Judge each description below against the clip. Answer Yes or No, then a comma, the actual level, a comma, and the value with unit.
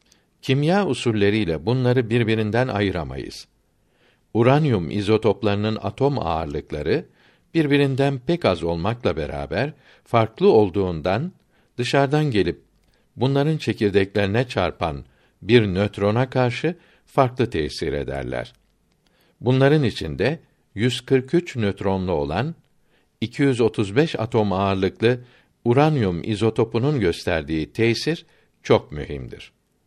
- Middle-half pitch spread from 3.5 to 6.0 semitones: Yes, wide, 5.5 semitones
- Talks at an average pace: No, slow, 80 wpm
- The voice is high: No, low, 115 Hz